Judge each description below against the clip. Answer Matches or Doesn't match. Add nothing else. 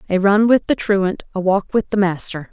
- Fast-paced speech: Matches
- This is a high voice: Matches